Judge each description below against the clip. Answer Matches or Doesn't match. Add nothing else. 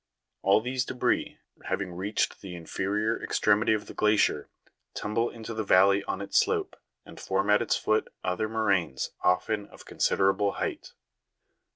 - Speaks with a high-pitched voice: Doesn't match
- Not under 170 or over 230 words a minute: Doesn't match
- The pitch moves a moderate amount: Doesn't match